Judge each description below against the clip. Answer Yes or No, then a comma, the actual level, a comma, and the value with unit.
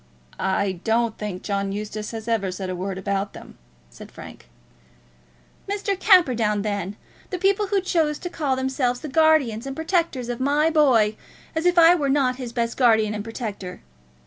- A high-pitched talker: Yes, high, 240 Hz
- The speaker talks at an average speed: Yes, average, 170 wpm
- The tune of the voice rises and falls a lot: Yes, wide, 7.0 semitones